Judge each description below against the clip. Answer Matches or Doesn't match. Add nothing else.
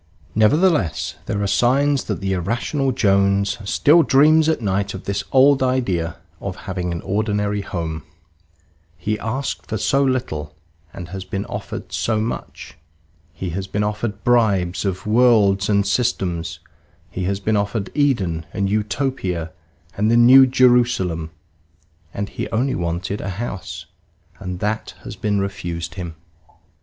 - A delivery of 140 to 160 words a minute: Matches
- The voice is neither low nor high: Doesn't match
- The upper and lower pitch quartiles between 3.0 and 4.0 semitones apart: Doesn't match